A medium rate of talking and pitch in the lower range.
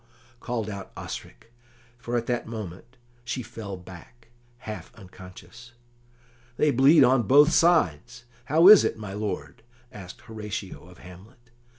No: slow, 130 wpm; low, 115 Hz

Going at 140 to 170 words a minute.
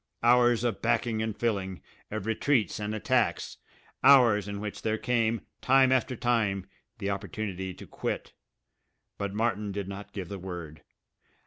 Yes: average, 145 wpm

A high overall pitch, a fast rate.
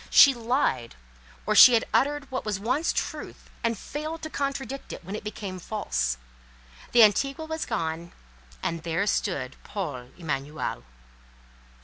No: high, 215 Hz; average, 140 wpm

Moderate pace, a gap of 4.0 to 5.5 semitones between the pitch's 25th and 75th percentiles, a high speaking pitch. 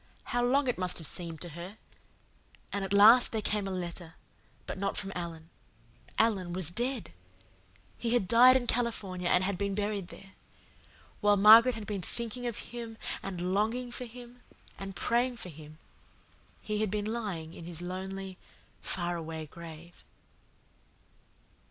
Yes: average, 155 wpm; average, 4.8 semitones; high, 195 Hz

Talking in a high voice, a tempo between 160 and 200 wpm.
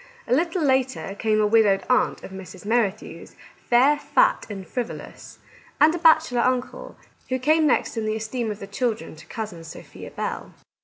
Yes: high, 235 Hz; average, 175 wpm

